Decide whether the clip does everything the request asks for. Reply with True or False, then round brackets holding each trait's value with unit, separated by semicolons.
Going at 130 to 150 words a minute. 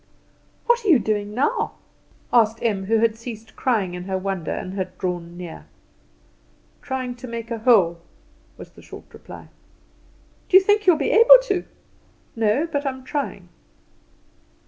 False (165 wpm)